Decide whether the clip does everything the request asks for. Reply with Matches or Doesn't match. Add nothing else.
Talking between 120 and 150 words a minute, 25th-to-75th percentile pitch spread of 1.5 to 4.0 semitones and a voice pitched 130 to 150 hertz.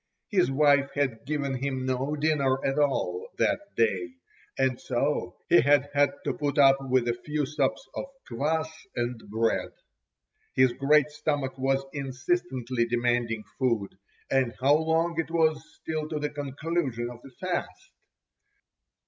Matches